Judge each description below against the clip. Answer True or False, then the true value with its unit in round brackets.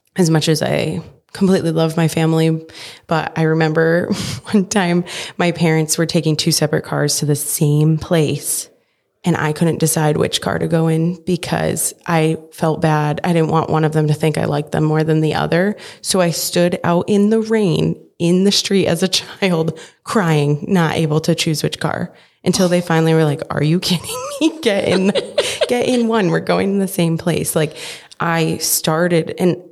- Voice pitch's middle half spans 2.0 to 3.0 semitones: True (2.5 semitones)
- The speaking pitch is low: False (165 Hz)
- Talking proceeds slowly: False (195 wpm)